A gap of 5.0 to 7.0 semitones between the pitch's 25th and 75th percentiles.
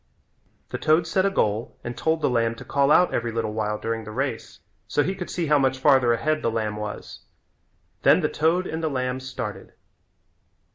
Yes: wide, 5.4 semitones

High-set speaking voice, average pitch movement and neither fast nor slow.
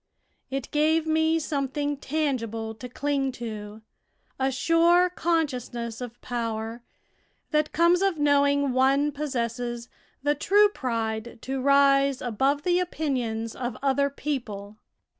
No: very high, 275 Hz; average, 4.0 semitones; slow, 120 wpm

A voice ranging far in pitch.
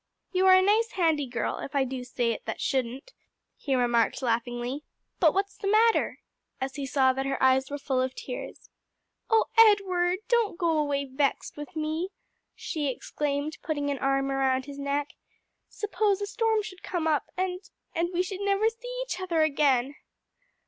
Yes: wide, 6.0 semitones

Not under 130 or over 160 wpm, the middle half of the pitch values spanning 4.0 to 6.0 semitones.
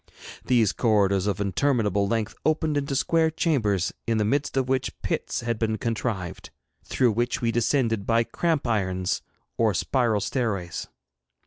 Yes: average, 145 wpm; average, 4.3 semitones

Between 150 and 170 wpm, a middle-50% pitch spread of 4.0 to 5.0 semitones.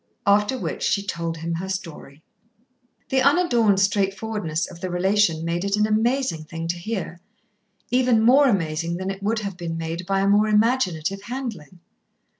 Yes: average, 165 wpm; average, 4.5 semitones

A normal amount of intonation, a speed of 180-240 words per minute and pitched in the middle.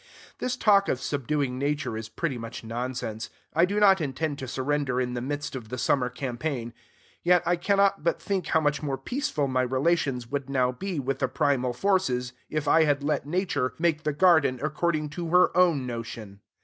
Yes: average, 5.0 semitones; average, 190 wpm; medium, 145 Hz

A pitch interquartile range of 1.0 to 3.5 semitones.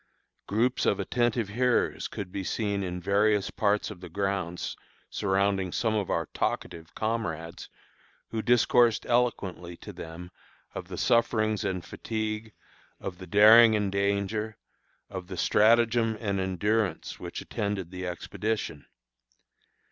Yes: average, 3.1 semitones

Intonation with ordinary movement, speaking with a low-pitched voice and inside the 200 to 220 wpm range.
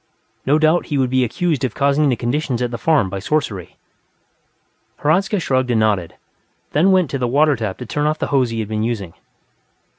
Yes: average, 4.9 semitones; low, 130 Hz; fast, 205 wpm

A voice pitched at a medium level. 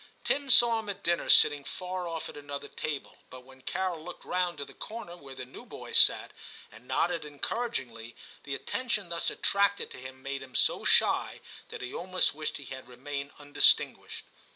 Yes: medium, 150 Hz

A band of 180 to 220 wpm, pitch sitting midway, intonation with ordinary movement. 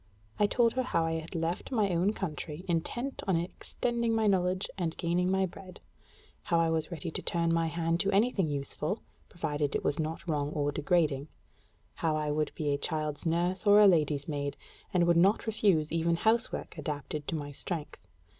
Yes: average, 190 wpm; medium, 170 Hz; average, 3.7 semitones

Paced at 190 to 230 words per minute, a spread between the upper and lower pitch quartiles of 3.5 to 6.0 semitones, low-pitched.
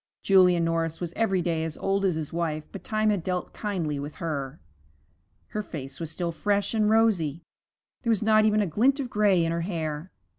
No: average, 200 wpm; average, 4.5 semitones; medium, 175 Hz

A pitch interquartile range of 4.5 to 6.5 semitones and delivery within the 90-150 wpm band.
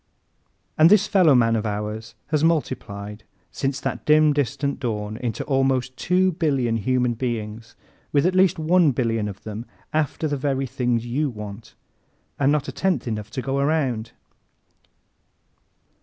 Yes: average, 5.2 semitones; average, 145 wpm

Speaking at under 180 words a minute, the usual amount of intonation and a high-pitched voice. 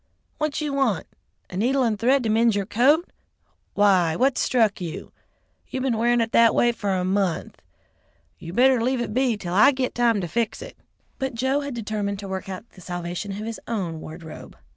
No: fast, 205 wpm; average, 4.8 semitones; high, 225 Hz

